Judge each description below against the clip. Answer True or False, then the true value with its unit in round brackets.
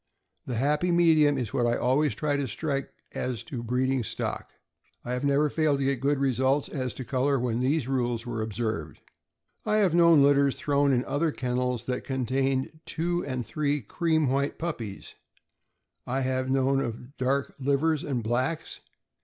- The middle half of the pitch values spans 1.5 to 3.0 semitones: True (2.7 semitones)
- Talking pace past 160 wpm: True (175 wpm)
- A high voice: False (135 Hz)